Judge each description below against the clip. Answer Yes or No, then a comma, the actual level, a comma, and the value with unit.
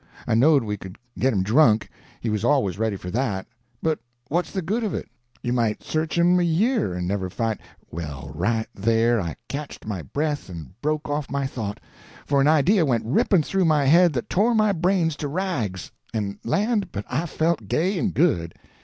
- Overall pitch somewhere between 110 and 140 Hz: Yes, low, 135 Hz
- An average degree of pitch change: No, wide, 8.0 semitones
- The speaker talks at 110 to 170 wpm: No, average, 185 wpm